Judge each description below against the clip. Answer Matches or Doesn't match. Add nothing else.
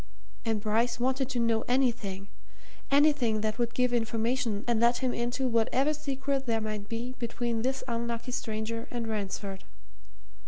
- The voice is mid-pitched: Doesn't match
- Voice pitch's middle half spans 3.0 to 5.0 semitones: Doesn't match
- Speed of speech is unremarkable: Matches